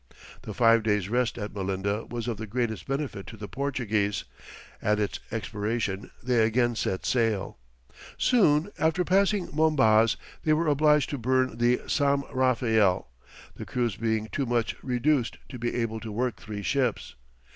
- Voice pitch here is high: No, low, 120 Hz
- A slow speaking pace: No, average, 155 wpm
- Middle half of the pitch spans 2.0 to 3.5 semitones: No, average, 4.0 semitones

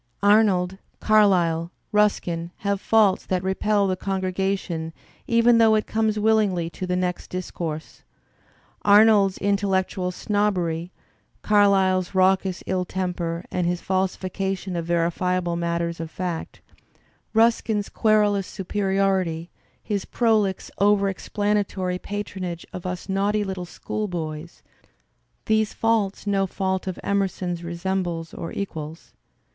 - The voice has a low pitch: No, high, 190 Hz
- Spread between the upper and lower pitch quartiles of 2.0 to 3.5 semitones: Yes, narrow, 2.5 semitones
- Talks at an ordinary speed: No, slow, 120 wpm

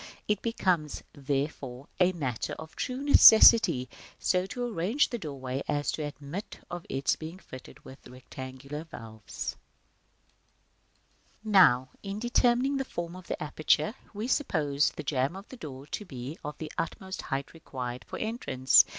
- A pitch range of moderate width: No, wide, 6.8 semitones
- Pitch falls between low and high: Yes, medium, 155 Hz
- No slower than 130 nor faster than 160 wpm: Yes, average, 155 wpm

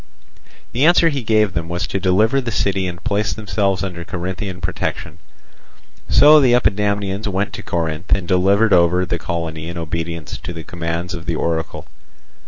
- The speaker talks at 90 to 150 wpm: No, average, 170 wpm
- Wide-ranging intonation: No, average, 3.4 semitones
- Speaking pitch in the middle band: No, very low, 90 Hz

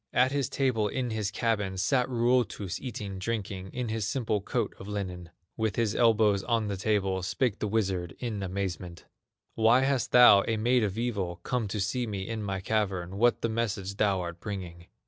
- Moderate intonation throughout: Yes, average, 3.3 semitones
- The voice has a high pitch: No, low, 105 Hz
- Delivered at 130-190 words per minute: Yes, average, 185 wpm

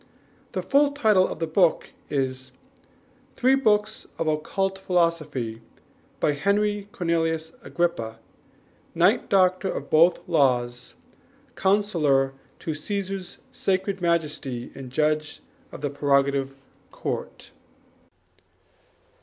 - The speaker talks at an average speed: No, slow, 100 wpm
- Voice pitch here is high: No, medium, 165 Hz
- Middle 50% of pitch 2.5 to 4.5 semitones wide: No, wide, 5.5 semitones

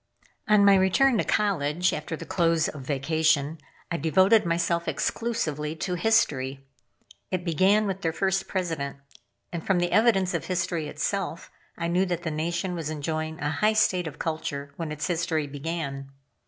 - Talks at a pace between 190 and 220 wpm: No, average, 165 wpm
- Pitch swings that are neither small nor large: Yes, average, 3.6 semitones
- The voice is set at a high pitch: No, medium, 170 Hz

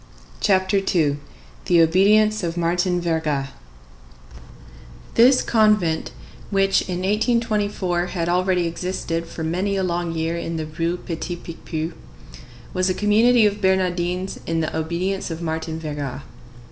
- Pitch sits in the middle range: Yes, medium, 175 Hz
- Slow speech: Yes, slow, 125 wpm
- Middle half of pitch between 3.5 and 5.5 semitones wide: No, average, 2.9 semitones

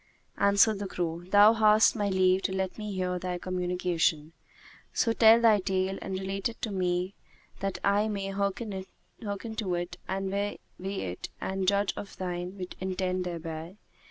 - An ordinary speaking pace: Yes, average, 155 wpm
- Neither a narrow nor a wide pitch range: No, narrow, 2.0 semitones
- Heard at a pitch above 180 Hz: Yes, high, 190 Hz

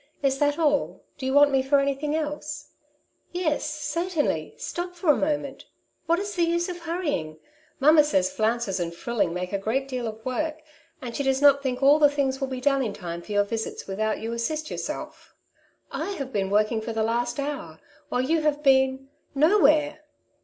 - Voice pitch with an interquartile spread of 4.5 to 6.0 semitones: Yes, average, 4.8 semitones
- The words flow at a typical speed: No, fast, 210 wpm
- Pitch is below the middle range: No, very high, 275 Hz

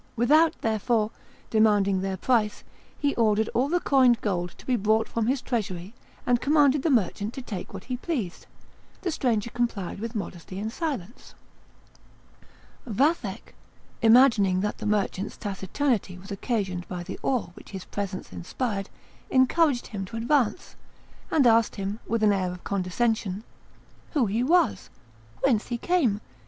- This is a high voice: Yes, high, 220 Hz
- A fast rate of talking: No, average, 150 wpm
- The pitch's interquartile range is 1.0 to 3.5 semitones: No, average, 4.4 semitones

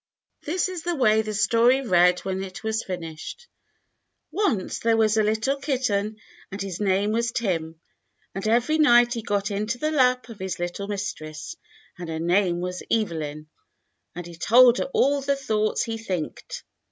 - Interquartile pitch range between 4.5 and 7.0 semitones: Yes, average, 4.9 semitones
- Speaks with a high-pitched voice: Yes, high, 215 Hz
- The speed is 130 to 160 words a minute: No, average, 175 wpm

